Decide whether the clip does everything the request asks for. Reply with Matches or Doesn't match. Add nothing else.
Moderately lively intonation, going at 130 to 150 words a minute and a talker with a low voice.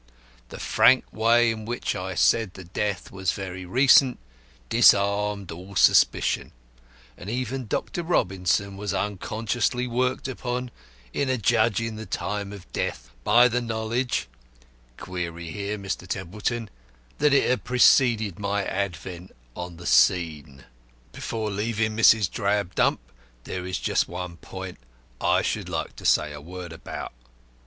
Matches